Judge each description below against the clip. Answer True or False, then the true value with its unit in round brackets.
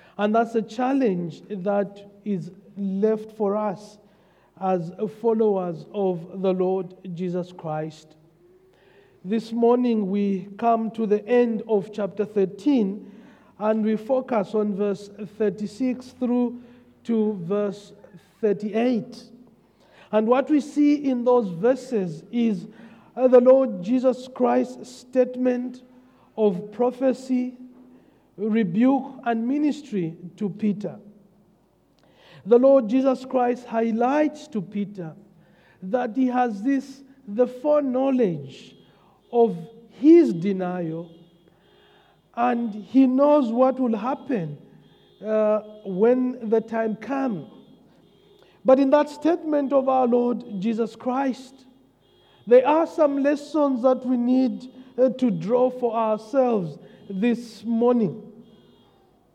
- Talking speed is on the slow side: True (105 wpm)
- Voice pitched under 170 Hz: False (225 Hz)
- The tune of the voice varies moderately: True (3.9 semitones)